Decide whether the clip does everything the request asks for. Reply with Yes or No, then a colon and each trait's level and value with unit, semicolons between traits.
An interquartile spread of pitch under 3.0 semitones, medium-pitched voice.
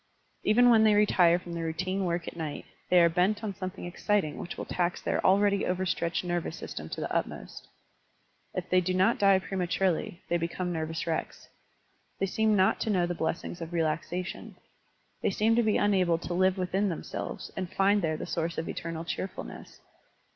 Yes: narrow, 2.6 semitones; medium, 180 Hz